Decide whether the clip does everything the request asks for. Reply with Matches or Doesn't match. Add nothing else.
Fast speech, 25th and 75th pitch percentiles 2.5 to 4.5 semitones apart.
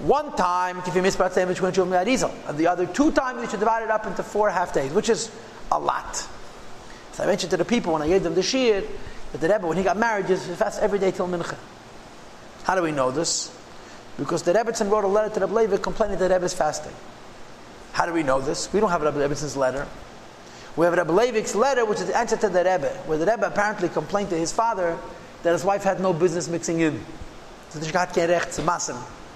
Matches